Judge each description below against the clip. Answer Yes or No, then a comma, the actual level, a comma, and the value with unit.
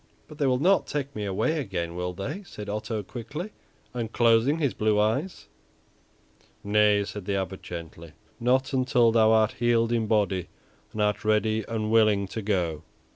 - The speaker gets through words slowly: No, average, 165 wpm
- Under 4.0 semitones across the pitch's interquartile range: Yes, average, 3.2 semitones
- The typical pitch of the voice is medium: No, low, 110 Hz